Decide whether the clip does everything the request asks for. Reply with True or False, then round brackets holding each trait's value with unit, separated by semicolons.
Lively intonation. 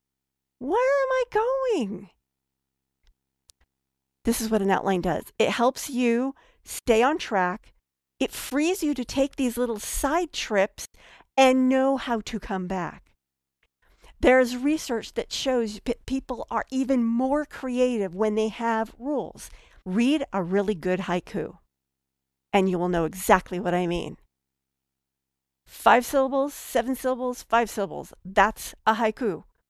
True (8.6 semitones)